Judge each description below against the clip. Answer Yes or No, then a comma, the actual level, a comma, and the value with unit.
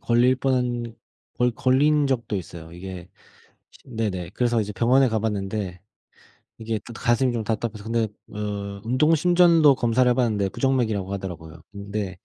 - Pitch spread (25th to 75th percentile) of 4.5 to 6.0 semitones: No, average, 4.0 semitones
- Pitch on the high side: No, low, 115 Hz